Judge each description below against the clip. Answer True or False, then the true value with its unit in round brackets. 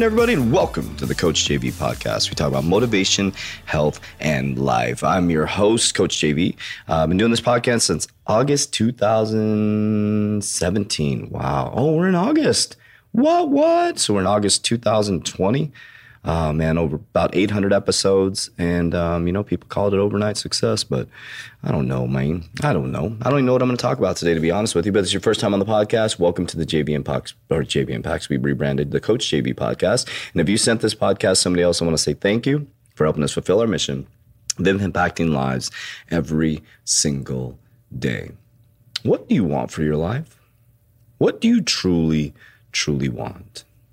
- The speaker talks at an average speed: True (195 wpm)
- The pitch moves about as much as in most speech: False (6.4 semitones)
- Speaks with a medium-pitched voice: False (100 Hz)